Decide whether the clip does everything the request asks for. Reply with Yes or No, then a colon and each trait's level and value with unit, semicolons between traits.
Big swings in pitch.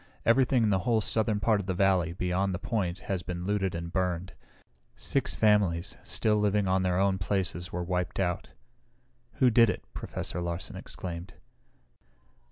No: average, 2.8 semitones